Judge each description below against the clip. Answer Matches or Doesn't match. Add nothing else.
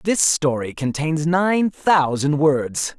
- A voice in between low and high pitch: Matches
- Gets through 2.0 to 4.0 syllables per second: Matches